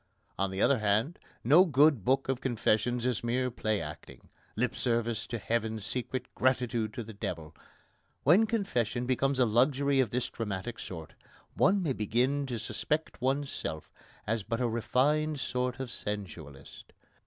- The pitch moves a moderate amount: Yes, average, 3.6 semitones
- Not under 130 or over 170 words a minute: Yes, average, 155 wpm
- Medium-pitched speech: No, low, 120 Hz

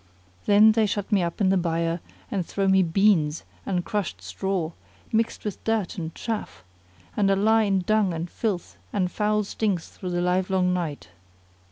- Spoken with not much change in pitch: No, average, 3.2 semitones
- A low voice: No, high, 190 Hz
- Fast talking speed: No, average, 175 wpm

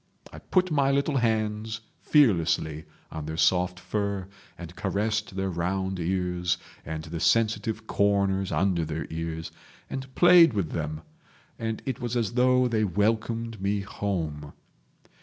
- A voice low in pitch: Yes, low, 100 Hz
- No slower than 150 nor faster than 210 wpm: No, average, 140 wpm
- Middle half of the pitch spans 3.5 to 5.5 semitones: Yes, average, 4.5 semitones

